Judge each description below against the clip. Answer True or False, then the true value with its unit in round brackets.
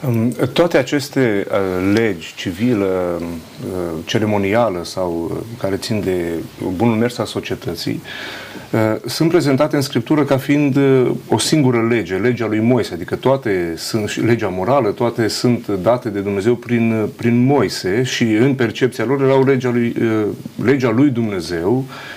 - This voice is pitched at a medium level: False (115 Hz)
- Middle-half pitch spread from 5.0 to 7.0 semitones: False (4.2 semitones)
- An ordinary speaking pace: True (145 wpm)